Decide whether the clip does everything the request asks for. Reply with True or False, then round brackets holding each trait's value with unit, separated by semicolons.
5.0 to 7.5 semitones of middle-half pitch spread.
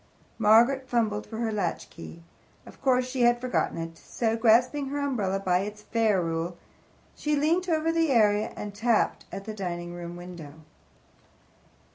True (5.6 semitones)